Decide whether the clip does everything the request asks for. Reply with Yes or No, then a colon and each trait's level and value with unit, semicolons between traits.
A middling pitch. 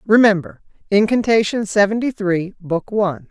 No: high, 205 Hz